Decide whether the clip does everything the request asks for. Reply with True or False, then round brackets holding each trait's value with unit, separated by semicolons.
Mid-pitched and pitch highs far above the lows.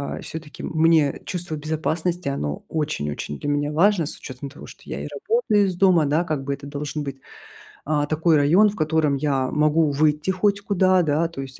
False (155 Hz; 3.1 semitones)